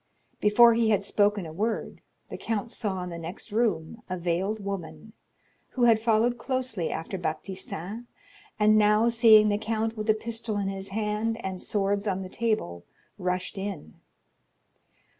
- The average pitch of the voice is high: Yes, high, 210 Hz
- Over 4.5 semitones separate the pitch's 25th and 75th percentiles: No, average, 2.8 semitones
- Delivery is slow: No, average, 160 wpm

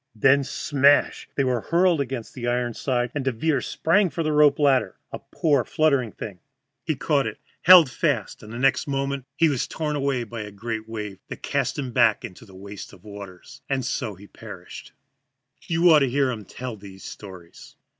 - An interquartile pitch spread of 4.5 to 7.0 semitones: Yes, average, 4.8 semitones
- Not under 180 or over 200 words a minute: Yes, average, 190 wpm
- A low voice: Yes, low, 130 Hz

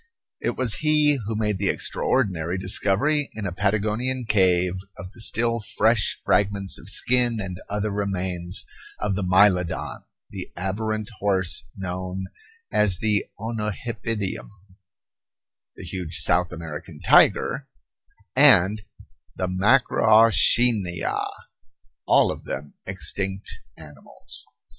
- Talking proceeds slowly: Yes, slow, 110 wpm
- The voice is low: Yes, low, 100 Hz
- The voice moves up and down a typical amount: Yes, average, 3.2 semitones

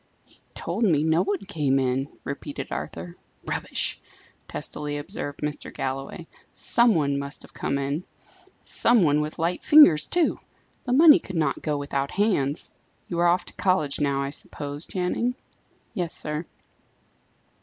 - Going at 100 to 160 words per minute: Yes, average, 150 wpm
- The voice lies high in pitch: No, medium, 150 Hz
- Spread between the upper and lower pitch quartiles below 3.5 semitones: No, average, 4.7 semitones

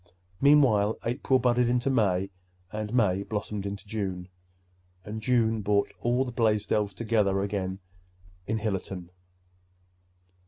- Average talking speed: No, slow, 115 wpm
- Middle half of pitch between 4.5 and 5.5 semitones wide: No, average, 3.2 semitones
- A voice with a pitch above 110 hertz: No, low, 105 Hz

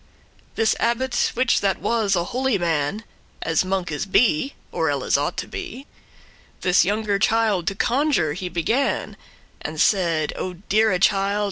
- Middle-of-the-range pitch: No, high, 200 Hz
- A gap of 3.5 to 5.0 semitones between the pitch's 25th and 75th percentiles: Yes, average, 4.6 semitones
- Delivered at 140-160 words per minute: Yes, average, 145 wpm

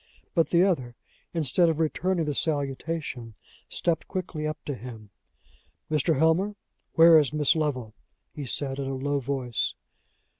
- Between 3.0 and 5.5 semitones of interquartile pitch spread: Yes, average, 3.6 semitones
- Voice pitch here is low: No, medium, 150 Hz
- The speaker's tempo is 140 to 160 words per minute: Yes, average, 145 wpm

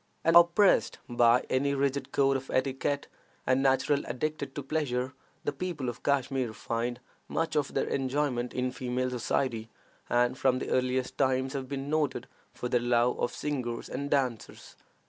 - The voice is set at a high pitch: No, low, 130 Hz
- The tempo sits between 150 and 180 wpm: Yes, average, 155 wpm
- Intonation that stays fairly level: Yes, narrow, 2.2 semitones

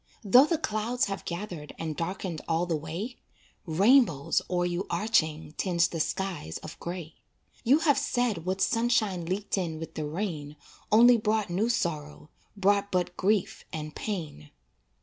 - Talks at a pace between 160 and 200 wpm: No, average, 150 wpm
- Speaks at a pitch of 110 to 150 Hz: No, medium, 185 Hz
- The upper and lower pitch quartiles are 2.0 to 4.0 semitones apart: No, average, 4.9 semitones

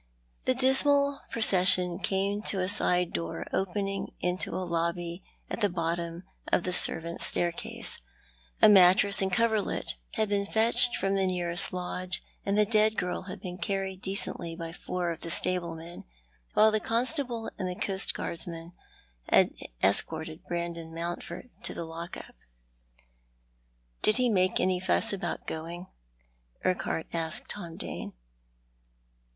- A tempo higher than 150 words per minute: No, average, 140 wpm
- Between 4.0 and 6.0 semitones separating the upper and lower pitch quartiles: No, average, 3.0 semitones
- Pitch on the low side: No, medium, 185 Hz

